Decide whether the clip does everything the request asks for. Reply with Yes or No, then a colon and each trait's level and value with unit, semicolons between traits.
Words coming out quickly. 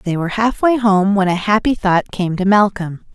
Yes: fast, 210 wpm